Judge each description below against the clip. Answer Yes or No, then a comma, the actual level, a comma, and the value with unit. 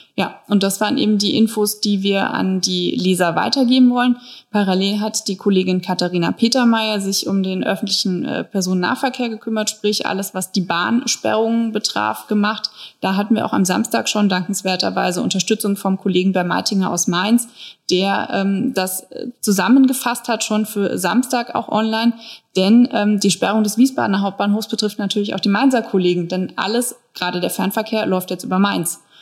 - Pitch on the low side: No, high, 205 Hz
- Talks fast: No, average, 165 wpm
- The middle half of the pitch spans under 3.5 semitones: Yes, average, 3.1 semitones